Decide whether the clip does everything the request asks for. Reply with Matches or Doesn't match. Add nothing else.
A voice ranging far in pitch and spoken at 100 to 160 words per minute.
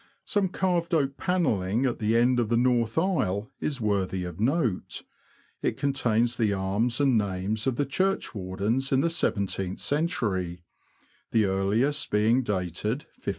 Matches